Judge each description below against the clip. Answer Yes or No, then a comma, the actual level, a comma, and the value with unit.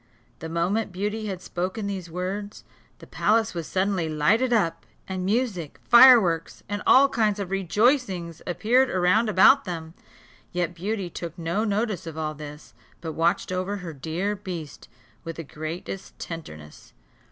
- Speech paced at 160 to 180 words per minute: No, average, 150 wpm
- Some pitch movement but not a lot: Yes, average, 4.0 semitones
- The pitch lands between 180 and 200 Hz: Yes, medium, 185 Hz